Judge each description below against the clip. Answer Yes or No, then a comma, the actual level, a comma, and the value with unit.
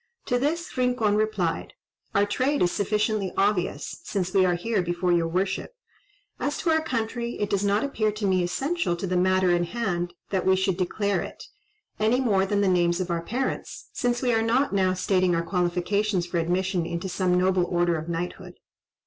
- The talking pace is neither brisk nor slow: Yes, average, 190 wpm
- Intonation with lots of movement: No, average, 3.6 semitones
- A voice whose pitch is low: No, high, 190 Hz